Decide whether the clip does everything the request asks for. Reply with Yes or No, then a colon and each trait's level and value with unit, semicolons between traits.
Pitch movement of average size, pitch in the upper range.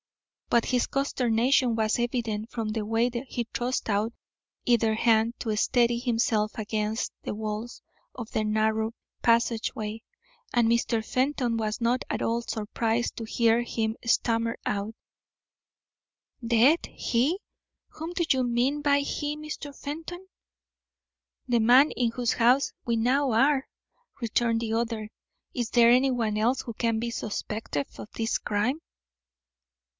No: narrow, 2.1 semitones; high, 235 Hz